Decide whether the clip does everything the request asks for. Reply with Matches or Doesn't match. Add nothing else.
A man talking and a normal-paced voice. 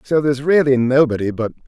Matches